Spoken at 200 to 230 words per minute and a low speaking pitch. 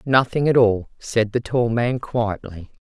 No: average, 170 wpm; low, 115 Hz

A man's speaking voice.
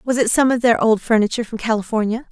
No: female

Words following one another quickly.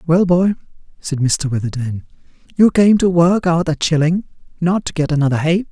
No: average, 170 wpm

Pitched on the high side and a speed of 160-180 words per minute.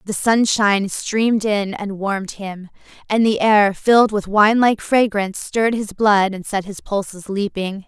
Yes: high, 205 Hz; average, 170 wpm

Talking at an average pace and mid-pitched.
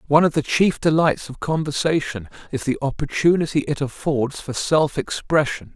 Yes: average, 155 wpm; medium, 145 Hz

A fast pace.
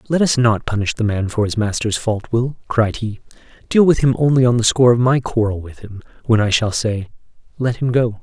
Yes: fast, 225 wpm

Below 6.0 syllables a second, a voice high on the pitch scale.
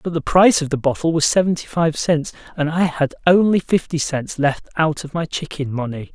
No: 5.3 syllables/s; medium, 155 Hz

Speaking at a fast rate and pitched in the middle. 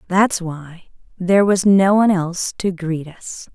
No: average, 170 wpm; medium, 180 Hz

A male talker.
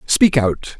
Yes: male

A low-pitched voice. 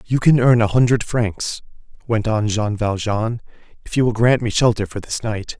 Yes: low, 110 Hz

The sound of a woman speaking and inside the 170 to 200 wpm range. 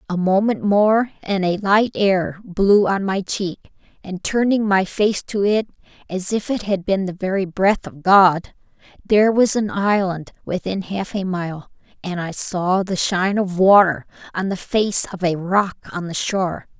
Yes: female; average, 180 wpm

